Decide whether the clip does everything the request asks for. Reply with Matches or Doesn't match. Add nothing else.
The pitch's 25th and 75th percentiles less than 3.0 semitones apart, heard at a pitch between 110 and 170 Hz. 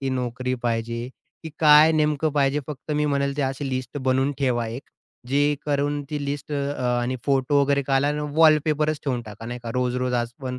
Matches